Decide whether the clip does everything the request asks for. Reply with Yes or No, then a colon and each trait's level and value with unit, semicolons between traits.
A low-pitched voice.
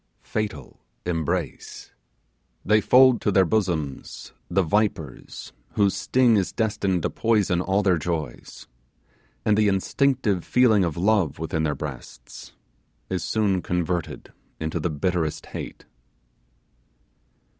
Yes: very low, 95 Hz